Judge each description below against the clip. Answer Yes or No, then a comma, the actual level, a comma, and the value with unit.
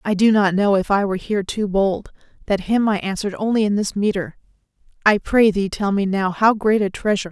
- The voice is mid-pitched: No, high, 200 Hz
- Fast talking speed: Yes, fast, 230 wpm